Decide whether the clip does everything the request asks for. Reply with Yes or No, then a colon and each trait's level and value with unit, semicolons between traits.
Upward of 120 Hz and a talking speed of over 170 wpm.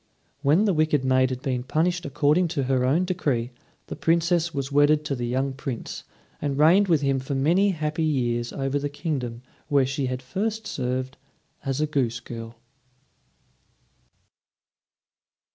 No: medium, 140 Hz; average, 155 wpm